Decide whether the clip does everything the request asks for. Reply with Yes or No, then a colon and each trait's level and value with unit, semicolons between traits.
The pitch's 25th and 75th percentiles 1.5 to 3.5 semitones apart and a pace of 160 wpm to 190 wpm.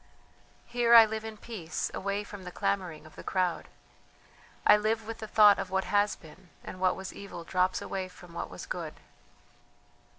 Yes: average, 2.8 semitones; average, 185 wpm